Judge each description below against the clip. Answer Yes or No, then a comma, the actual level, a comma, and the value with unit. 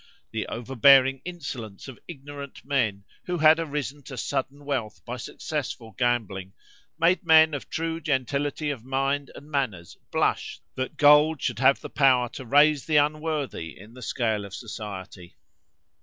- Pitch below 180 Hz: Yes, low, 135 Hz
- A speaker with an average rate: Yes, average, 150 wpm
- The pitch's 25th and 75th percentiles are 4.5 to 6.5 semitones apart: No, average, 4.0 semitones